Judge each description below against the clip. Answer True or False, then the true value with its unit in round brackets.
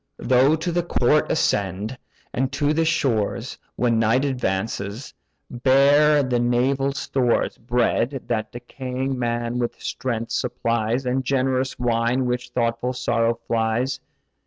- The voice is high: False (125 Hz)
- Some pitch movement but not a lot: False (2.2 semitones)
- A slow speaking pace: True (125 wpm)